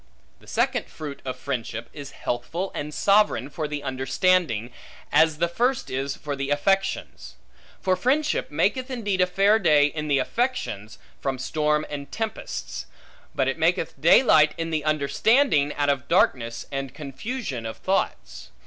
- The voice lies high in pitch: No, medium, 150 Hz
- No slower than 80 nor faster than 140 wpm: No, average, 150 wpm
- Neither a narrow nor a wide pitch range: No, wide, 5.7 semitones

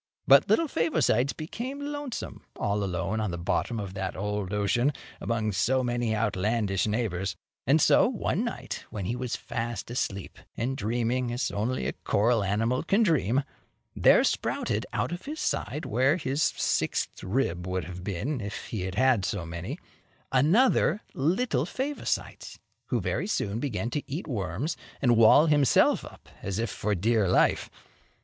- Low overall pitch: Yes, low, 115 Hz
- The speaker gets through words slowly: No, average, 160 wpm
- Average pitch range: No, wide, 5.8 semitones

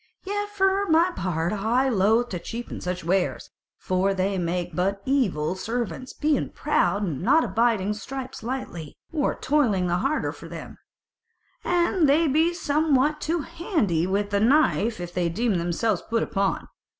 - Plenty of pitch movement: Yes, wide, 8.2 semitones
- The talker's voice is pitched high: Yes, high, 225 Hz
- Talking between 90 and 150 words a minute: No, average, 160 wpm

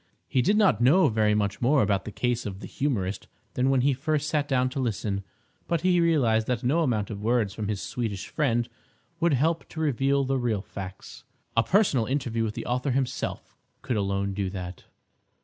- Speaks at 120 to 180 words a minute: No, average, 200 wpm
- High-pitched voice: No, low, 125 Hz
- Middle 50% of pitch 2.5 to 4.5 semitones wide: No, average, 5.1 semitones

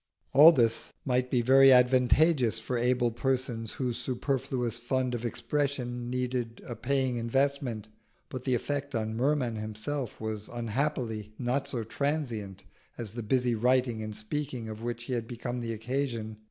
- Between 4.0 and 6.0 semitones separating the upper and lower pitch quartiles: No, narrow, 2.5 semitones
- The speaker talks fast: No, average, 155 wpm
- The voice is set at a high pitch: No, low, 125 Hz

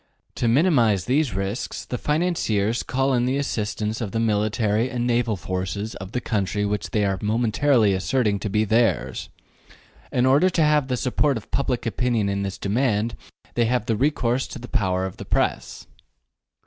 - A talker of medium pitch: No, low, 115 Hz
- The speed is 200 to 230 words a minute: No, average, 175 wpm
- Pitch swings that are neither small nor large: Yes, average, 3.7 semitones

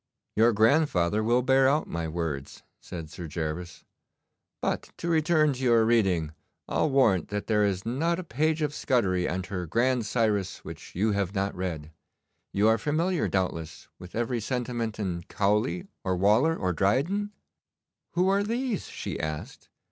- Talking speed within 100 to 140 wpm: No, average, 160 wpm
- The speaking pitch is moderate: No, low, 110 Hz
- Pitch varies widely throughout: Yes, wide, 7.0 semitones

